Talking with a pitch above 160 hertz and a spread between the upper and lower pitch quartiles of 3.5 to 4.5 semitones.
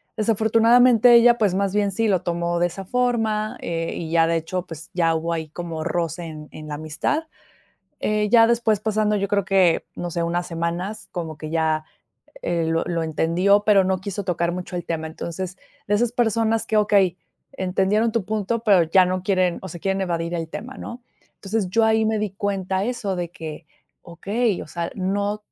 Yes: high, 190 Hz; average, 4.1 semitones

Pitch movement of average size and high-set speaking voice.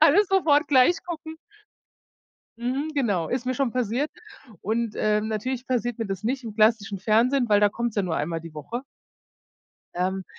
Yes: average, 4.3 semitones; high, 235 Hz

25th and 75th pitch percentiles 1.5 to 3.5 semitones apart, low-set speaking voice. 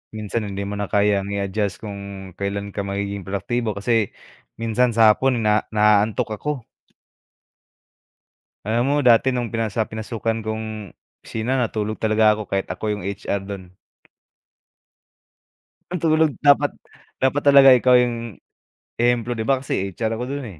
Yes: average, 3.1 semitones; low, 110 Hz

